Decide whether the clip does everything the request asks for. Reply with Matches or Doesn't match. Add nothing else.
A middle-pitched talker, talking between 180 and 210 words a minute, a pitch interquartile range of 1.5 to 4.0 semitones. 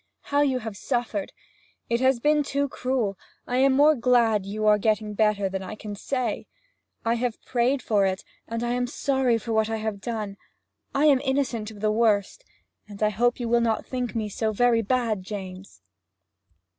Doesn't match